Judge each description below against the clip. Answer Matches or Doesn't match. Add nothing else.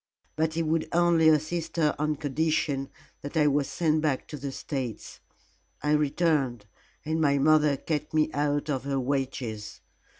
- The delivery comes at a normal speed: Matches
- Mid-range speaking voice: Matches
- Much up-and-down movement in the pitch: Doesn't match